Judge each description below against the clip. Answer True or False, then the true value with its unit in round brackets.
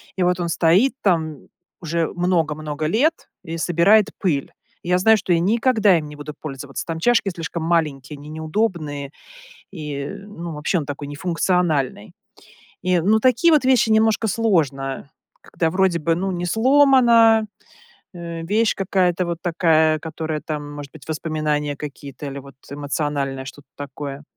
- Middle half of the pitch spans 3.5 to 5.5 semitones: True (4.5 semitones)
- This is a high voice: False (165 Hz)